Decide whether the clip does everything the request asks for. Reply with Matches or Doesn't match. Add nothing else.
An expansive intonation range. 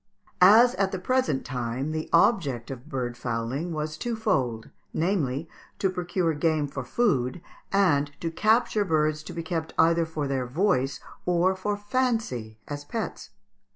Matches